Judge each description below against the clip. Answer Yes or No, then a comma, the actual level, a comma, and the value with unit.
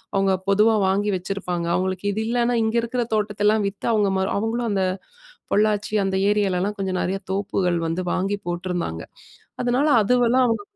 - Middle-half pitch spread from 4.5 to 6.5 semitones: No, average, 2.7 semitones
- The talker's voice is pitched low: No, high, 200 Hz